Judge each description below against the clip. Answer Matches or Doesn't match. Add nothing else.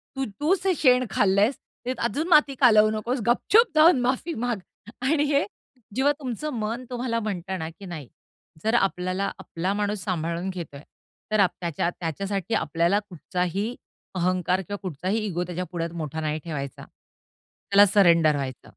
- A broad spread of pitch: Matches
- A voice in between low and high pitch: Doesn't match